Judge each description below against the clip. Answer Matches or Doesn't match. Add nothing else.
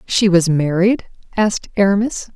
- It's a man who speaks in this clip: Doesn't match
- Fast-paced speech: Doesn't match